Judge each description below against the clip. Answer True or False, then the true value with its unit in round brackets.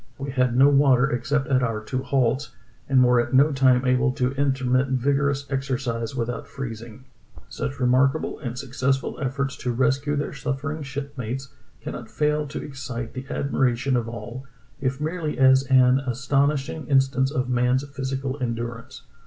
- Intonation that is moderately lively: False (1.8 semitones)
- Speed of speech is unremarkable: True (155 wpm)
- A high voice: False (130 Hz)